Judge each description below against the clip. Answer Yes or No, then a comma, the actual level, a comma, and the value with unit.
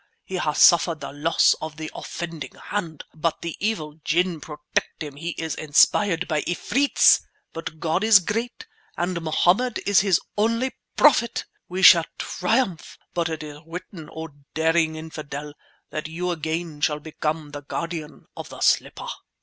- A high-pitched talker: No, medium, 165 Hz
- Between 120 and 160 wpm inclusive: Yes, average, 155 wpm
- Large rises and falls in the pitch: No, average, 2.8 semitones